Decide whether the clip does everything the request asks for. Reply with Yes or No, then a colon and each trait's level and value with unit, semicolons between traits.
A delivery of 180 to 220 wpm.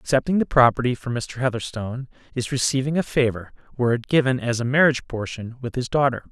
Yes: average, 190 wpm